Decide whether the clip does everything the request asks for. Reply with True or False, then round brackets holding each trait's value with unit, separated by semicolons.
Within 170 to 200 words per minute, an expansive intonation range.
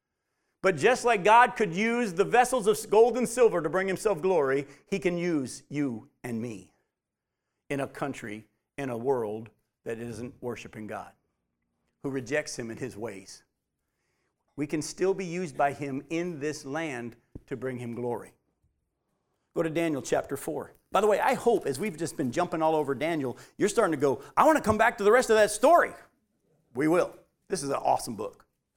True (190 wpm; 9.0 semitones)